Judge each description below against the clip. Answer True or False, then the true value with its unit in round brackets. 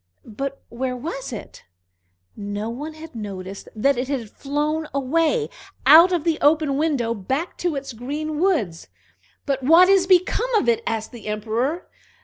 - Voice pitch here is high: True (275 Hz)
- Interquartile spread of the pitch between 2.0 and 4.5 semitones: False (5.5 semitones)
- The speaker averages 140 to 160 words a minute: True (155 wpm)